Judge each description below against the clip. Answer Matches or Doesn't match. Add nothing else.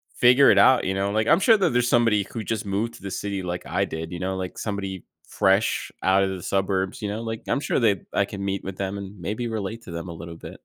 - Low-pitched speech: Matches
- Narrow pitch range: Doesn't match